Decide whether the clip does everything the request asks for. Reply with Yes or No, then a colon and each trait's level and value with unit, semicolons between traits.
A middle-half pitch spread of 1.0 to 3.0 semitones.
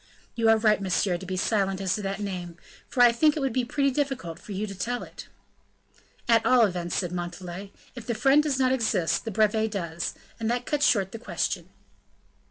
No: average, 4.6 semitones